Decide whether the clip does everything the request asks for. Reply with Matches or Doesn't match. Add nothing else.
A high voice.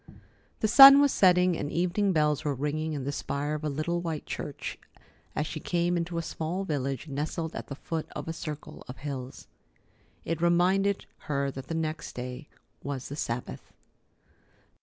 Doesn't match